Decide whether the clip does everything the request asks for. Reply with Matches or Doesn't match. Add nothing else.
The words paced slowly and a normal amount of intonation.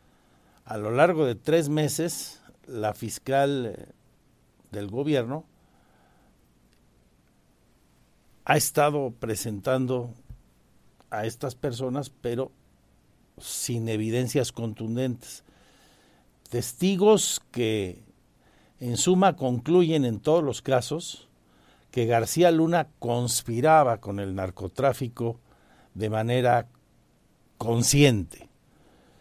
Matches